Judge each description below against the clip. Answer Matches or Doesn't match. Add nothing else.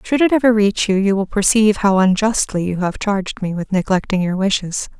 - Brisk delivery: Matches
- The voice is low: Doesn't match